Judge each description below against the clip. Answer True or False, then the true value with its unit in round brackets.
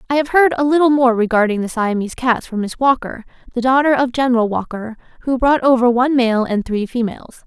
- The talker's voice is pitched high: True (245 Hz)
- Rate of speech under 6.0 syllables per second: False (6.1 syllables/s)